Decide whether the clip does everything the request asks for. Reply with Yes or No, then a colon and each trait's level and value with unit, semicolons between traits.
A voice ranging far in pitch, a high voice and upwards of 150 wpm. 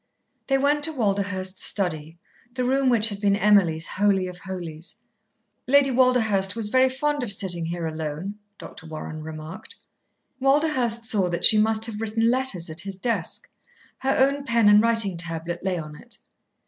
Yes: wide, 6.0 semitones; high, 205 Hz; average, 165 wpm